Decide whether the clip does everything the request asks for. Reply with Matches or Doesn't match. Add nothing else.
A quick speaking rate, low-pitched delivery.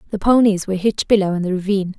Doesn't match